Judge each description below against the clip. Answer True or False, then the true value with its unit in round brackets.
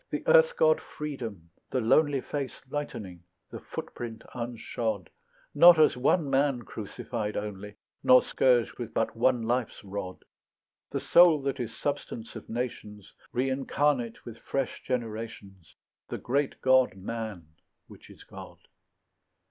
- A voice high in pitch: False (120 Hz)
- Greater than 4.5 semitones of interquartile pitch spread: False (4.1 semitones)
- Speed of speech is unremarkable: False (130 wpm)